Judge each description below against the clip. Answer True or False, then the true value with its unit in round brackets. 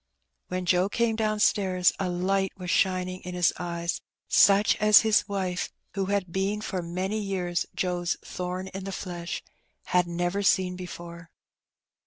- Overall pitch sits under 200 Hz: True (185 Hz)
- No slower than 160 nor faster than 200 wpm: False (150 wpm)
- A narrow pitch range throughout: True (1.7 semitones)